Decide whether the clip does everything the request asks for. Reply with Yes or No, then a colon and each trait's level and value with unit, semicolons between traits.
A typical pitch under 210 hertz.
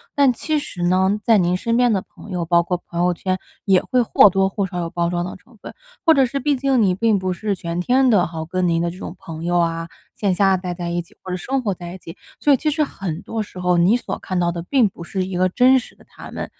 Yes: medium, 185 Hz